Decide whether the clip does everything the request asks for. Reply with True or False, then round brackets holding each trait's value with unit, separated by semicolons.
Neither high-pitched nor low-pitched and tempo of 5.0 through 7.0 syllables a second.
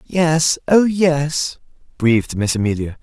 False (145 Hz; 3.7 syllables/s)